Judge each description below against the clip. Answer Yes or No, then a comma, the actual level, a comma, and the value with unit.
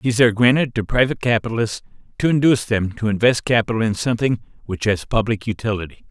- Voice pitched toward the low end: Yes, low, 115 Hz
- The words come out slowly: No, average, 175 wpm